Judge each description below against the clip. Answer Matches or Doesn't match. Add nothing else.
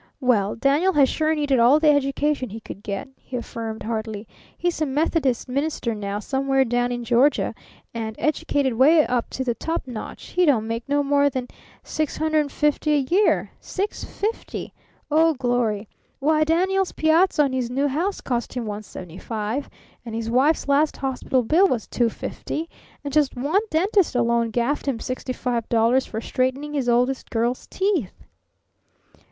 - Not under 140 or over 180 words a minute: Matches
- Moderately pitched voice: Doesn't match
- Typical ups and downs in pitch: Matches